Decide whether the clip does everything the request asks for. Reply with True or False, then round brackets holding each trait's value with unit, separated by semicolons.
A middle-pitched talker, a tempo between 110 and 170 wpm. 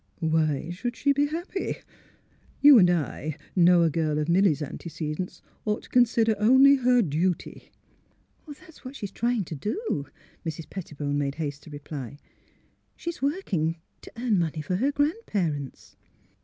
True (180 Hz; 160 wpm)